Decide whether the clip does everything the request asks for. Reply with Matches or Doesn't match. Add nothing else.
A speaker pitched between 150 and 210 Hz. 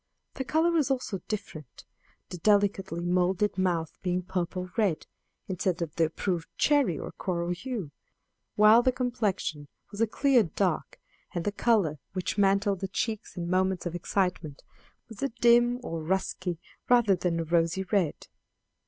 Matches